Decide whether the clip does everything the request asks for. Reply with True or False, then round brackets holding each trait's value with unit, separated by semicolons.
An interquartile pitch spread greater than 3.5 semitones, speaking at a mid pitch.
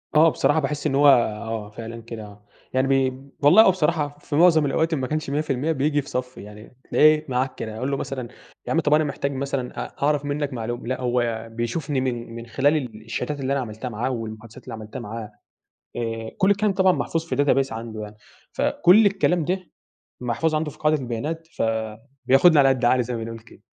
False (4.5 semitones; 130 Hz)